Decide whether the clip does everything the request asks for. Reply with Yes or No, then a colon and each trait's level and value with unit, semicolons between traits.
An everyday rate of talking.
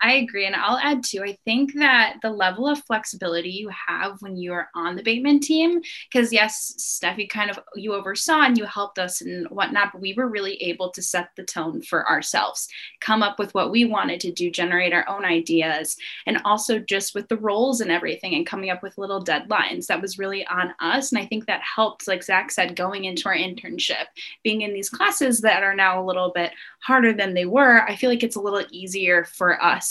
No: fast, 225 wpm